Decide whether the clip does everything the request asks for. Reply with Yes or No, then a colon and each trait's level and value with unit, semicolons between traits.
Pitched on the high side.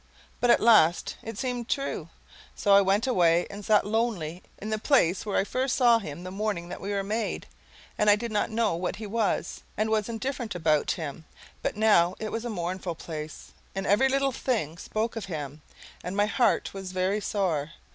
Yes: high, 205 Hz